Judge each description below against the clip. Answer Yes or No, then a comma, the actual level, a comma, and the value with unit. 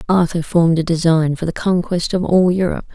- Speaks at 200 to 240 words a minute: Yes, fast, 205 wpm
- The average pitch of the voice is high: No, medium, 170 Hz